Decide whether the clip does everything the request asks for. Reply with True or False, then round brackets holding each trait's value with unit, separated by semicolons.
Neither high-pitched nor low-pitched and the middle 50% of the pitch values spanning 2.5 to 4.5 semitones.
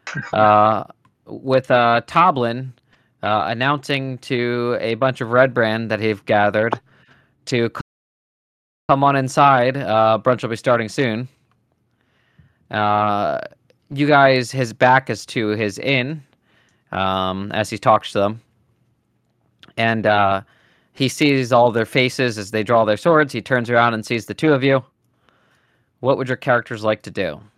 False (120 Hz; 3.2 semitones)